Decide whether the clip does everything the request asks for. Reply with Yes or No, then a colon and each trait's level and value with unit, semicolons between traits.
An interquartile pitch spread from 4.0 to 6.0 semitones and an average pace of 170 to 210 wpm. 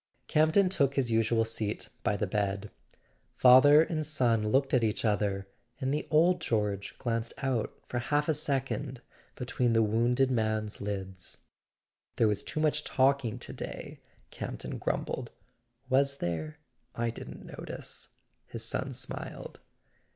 No: average, 4.5 semitones; average, 145 wpm